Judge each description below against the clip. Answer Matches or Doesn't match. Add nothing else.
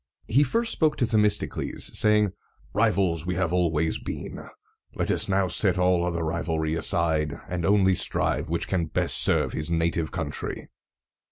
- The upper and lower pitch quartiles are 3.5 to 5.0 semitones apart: Matches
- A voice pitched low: Matches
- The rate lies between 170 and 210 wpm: Doesn't match